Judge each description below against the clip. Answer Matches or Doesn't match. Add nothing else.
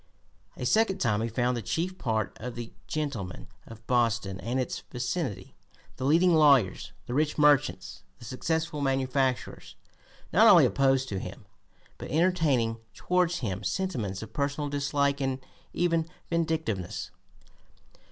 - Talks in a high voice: Doesn't match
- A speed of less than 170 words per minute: Matches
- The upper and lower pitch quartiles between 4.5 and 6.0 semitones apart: Matches